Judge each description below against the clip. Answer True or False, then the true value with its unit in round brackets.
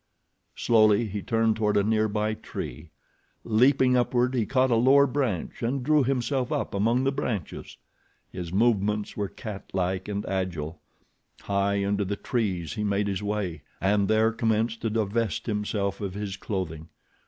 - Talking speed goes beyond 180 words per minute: False (155 wpm)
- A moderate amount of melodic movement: True (3.0 semitones)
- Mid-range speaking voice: False (105 Hz)